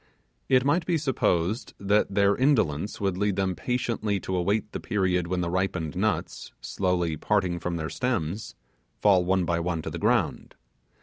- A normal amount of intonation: Yes, average, 3.4 semitones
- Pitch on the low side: Yes, very low, 95 Hz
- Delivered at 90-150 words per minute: No, average, 170 wpm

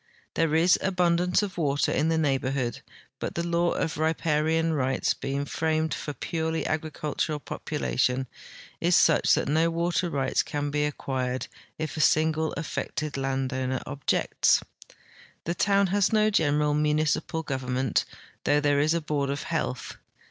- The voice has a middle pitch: Yes, medium, 155 Hz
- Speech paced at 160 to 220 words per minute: No, average, 150 wpm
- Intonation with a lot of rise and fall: No, average, 2.8 semitones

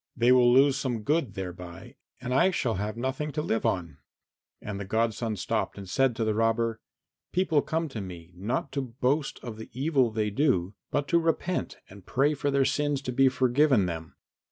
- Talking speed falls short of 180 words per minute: No, average, 195 wpm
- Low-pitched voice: Yes, low, 120 Hz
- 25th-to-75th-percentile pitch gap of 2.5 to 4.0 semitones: No, average, 4.8 semitones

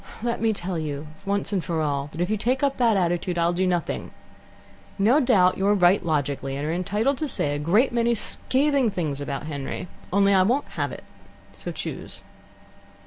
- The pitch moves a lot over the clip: Yes, wide, 6.2 semitones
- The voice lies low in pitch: No, medium, 185 Hz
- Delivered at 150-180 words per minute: No, average, 190 wpm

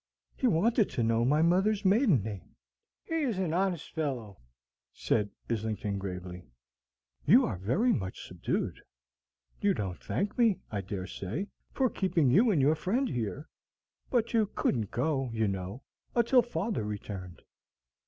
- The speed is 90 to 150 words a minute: Yes, average, 145 wpm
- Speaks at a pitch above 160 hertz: No, medium, 145 Hz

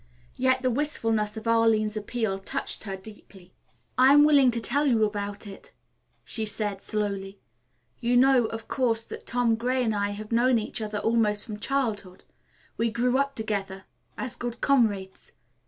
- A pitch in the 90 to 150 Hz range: No, high, 225 Hz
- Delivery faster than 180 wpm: No, average, 165 wpm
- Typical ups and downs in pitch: Yes, average, 3.1 semitones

